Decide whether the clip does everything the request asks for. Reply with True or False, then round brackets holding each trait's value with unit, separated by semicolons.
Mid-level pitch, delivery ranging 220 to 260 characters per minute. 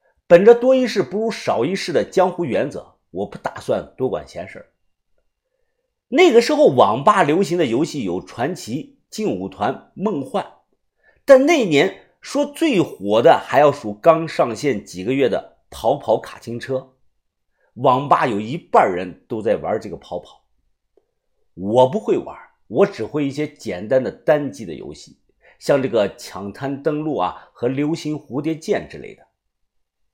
True (160 Hz; 225 characters per minute)